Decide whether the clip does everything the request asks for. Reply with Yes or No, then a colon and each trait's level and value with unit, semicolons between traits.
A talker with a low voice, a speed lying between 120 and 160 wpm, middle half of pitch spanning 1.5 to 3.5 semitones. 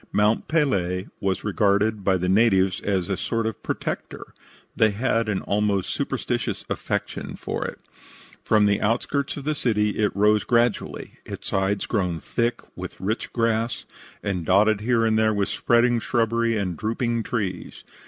Yes: low, 105 Hz; average, 155 wpm; average, 2.8 semitones